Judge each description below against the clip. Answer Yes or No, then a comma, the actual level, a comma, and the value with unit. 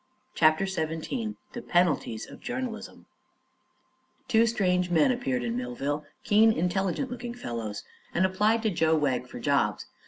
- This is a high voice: No, medium, 180 Hz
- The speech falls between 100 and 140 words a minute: Yes, slow, 135 wpm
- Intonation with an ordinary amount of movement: No, wide, 7.0 semitones